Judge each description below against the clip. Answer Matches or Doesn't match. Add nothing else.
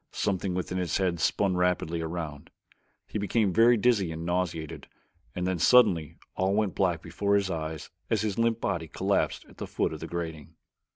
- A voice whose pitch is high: Doesn't match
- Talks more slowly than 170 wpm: Doesn't match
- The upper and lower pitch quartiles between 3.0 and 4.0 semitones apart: Matches